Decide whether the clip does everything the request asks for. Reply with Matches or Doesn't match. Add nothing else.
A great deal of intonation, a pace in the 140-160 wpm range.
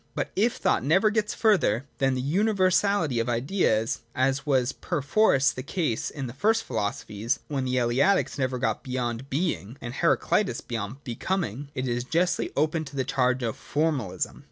Doesn't match